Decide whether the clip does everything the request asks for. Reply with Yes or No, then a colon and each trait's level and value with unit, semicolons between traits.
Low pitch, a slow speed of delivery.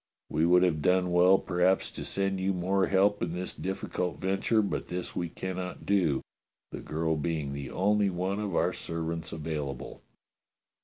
No: very low, 90 Hz; average, 165 wpm